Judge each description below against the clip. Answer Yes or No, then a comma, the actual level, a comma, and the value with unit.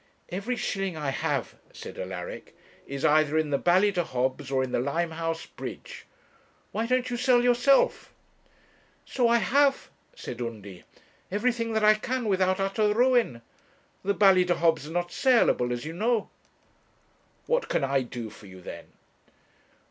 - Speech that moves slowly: No, average, 145 wpm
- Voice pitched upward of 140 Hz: Yes, medium, 185 Hz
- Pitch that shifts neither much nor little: No, wide, 9.0 semitones